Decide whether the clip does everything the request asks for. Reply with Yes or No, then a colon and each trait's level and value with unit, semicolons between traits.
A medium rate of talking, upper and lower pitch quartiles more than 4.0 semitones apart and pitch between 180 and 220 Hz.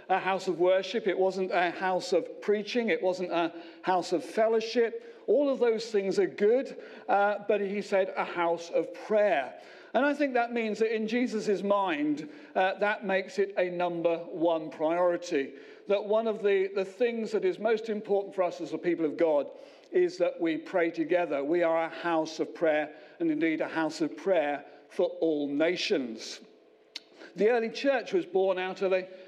Yes: average, 195 wpm; average, 4.6 semitones; high, 190 Hz